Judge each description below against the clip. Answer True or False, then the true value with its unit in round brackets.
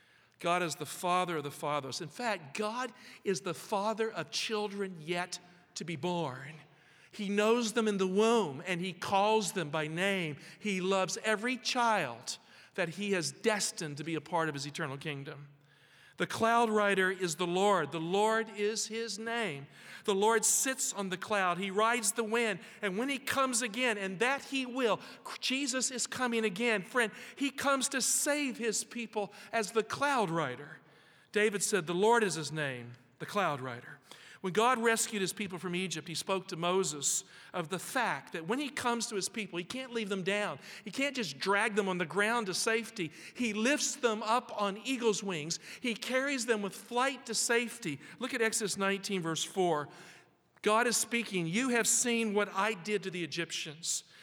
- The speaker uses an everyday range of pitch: True (4.6 semitones)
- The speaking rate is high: False (190 wpm)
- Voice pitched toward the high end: True (205 Hz)